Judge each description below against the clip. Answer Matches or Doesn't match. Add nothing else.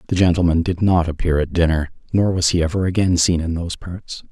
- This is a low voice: Matches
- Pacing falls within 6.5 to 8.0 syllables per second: Doesn't match